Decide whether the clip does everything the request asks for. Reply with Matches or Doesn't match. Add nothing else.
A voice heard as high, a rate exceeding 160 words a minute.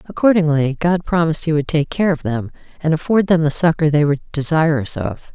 Doesn't match